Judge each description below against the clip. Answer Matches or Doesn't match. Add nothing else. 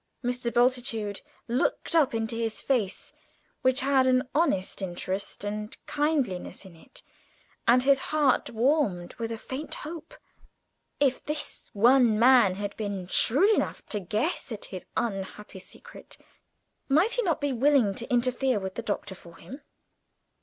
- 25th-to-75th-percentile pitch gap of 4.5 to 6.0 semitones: Matches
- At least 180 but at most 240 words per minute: Doesn't match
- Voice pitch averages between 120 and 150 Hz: Doesn't match